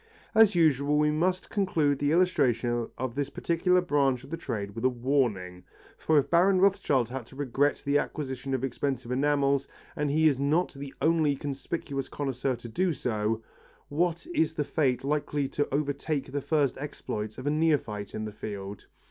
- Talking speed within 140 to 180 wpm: Yes, average, 175 wpm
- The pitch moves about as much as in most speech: Yes, average, 3.5 semitones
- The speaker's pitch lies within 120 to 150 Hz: Yes, medium, 140 Hz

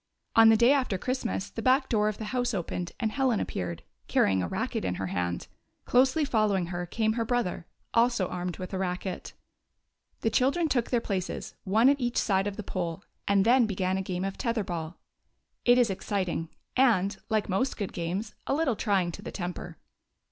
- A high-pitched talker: Yes, high, 205 Hz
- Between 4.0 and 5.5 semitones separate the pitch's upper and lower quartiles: Yes, average, 5.0 semitones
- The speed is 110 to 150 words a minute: No, average, 195 wpm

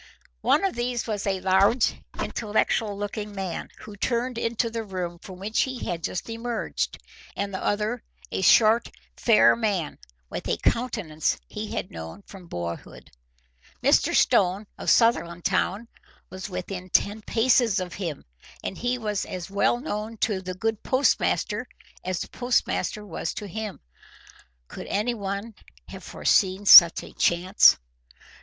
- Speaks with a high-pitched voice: Yes, high, 205 Hz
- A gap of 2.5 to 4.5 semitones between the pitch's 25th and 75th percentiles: Yes, average, 3.6 semitones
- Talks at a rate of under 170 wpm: Yes, average, 145 wpm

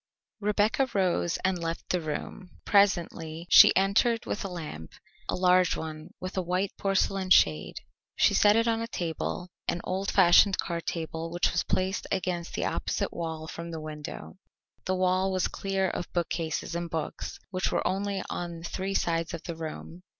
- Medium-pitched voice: Yes, medium, 180 Hz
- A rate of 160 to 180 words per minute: Yes, average, 170 wpm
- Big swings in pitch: No, narrow, 2.6 semitones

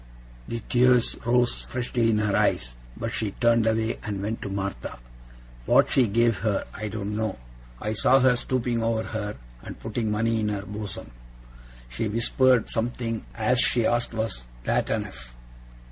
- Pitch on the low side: Yes, low, 110 Hz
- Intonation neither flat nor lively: No, narrow, 2.1 semitones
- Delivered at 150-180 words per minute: Yes, average, 160 wpm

